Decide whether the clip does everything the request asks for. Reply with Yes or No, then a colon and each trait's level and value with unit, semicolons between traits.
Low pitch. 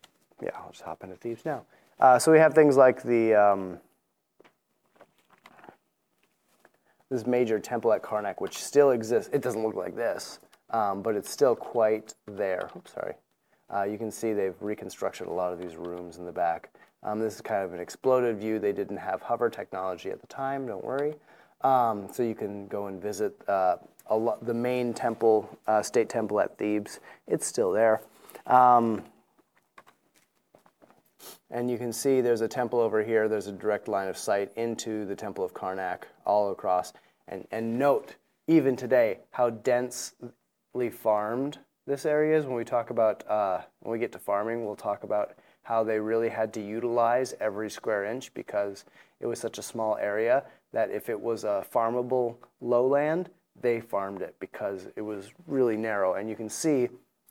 Yes: low, 115 Hz